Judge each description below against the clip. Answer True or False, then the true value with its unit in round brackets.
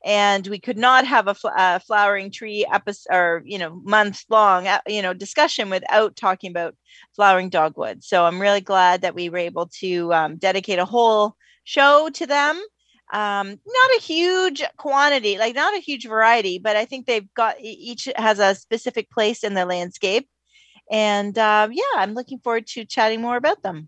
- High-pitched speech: True (210 Hz)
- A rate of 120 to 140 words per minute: False (185 wpm)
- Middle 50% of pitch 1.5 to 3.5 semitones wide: False (4.0 semitones)